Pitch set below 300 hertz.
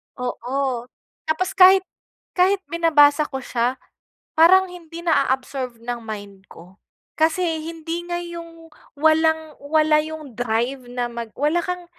No: very high, 305 Hz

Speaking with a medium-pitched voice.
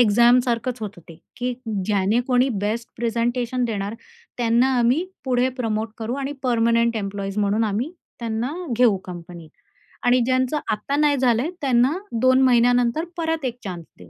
No: high, 235 Hz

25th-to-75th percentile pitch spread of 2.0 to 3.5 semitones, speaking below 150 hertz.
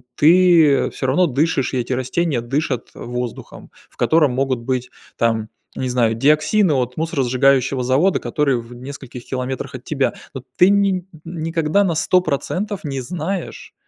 No: average, 4.6 semitones; medium, 140 Hz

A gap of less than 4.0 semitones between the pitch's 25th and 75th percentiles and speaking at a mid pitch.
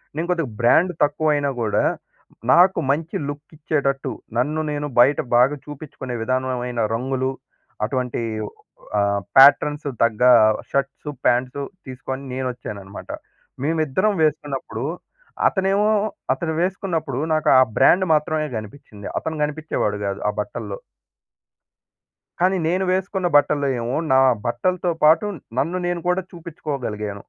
No: average, 4.3 semitones; medium, 145 Hz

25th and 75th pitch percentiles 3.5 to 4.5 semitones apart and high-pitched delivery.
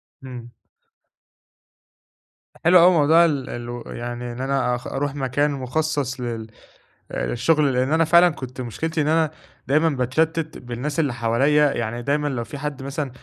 No: average, 3.8 semitones; medium, 140 Hz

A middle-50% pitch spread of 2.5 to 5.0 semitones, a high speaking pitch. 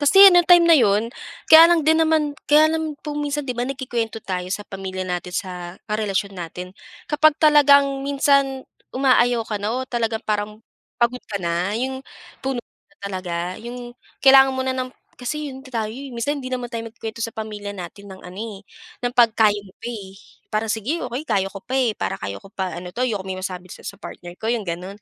No: wide, 5.5 semitones; high, 230 Hz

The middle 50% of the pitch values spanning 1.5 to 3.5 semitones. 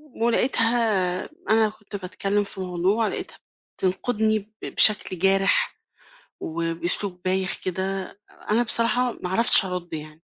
Yes: average, 3.1 semitones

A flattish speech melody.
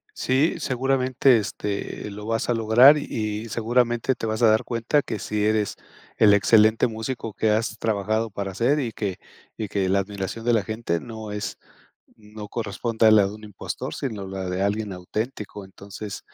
Yes: narrow, 2.2 semitones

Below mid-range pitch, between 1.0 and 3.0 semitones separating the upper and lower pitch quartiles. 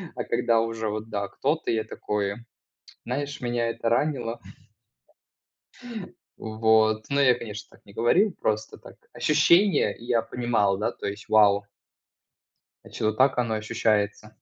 Yes: low, 115 Hz; narrow, 2.4 semitones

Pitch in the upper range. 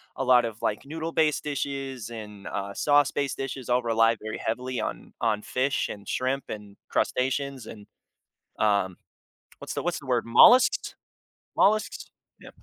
No: low, 125 Hz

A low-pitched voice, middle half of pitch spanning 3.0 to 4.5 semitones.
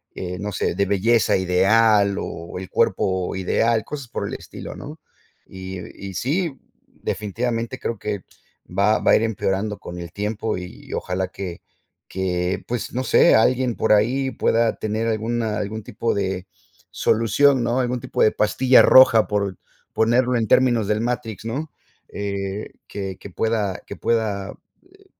Yes: low, 110 Hz; average, 3.4 semitones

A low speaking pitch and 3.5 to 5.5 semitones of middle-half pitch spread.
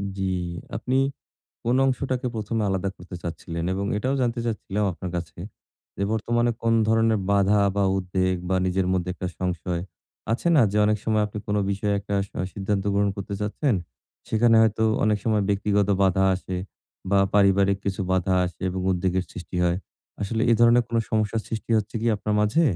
No: low, 100 Hz; average, 3.0 semitones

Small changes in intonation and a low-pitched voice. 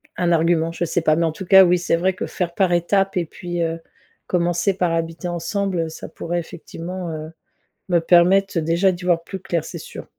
No: narrow, 1.7 semitones; medium, 175 Hz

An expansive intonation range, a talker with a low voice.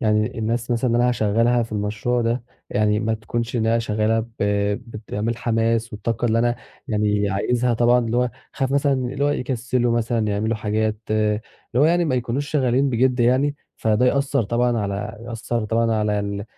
No: narrow, 2.4 semitones; low, 115 Hz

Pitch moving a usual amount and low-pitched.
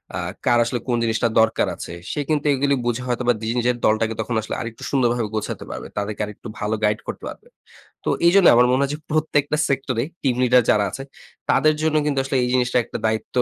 Yes: average, 3.6 semitones; low, 125 Hz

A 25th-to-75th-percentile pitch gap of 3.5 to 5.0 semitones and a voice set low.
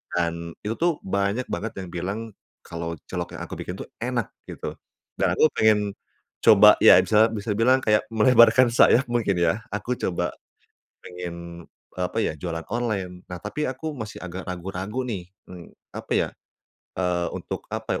Yes: average, 4.7 semitones; low, 100 Hz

